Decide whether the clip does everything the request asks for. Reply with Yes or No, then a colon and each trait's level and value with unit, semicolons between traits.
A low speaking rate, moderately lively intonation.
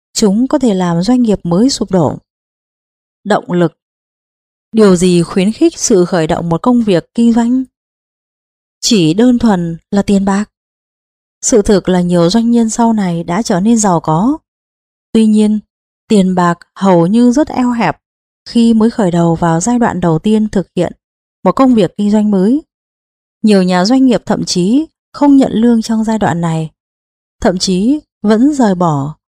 No: average, 175 wpm; average, 5.0 semitones